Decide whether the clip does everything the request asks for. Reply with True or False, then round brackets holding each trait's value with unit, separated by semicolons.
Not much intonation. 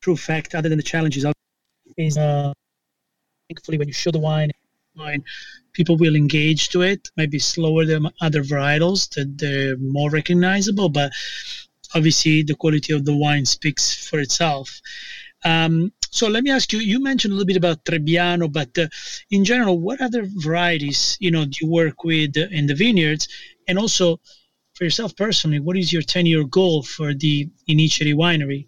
False (3.2 semitones)